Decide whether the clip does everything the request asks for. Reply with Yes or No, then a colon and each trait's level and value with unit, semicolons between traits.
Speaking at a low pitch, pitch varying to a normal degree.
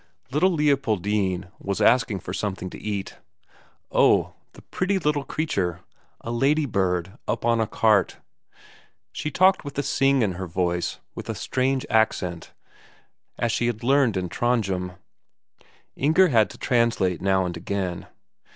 No: low, 110 Hz; wide, 6.4 semitones